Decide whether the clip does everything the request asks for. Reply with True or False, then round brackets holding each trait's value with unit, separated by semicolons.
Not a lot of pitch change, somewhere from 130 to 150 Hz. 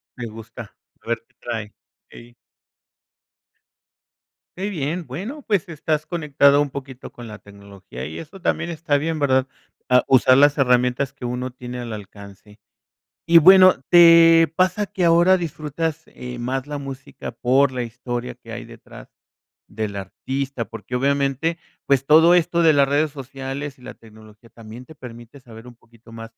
False (4.9 semitones; 135 Hz)